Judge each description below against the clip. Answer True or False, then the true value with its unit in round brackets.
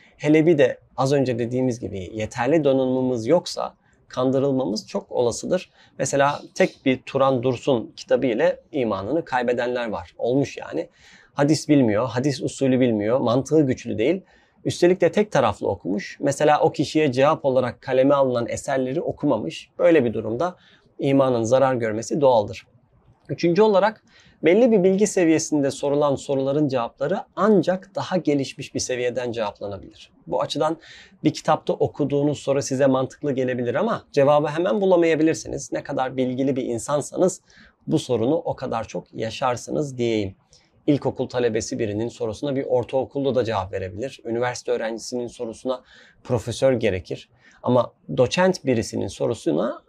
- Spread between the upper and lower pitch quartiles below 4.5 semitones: True (3.4 semitones)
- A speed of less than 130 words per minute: False (135 wpm)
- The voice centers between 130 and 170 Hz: True (135 Hz)